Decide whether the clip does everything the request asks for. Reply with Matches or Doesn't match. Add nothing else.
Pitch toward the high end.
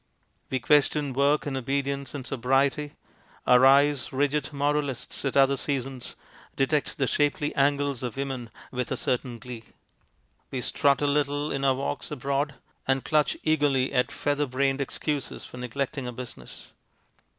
Doesn't match